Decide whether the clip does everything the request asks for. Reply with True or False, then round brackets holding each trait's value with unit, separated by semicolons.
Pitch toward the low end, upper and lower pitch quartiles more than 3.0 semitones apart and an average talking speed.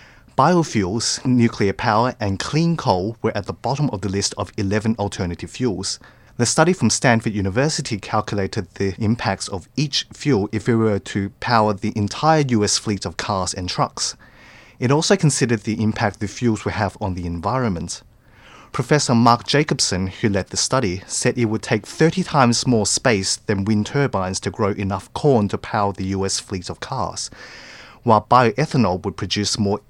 True (110 Hz; 3.7 semitones; 175 wpm)